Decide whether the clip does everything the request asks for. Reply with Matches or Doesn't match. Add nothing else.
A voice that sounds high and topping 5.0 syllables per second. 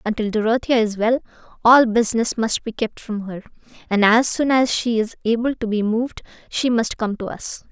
Matches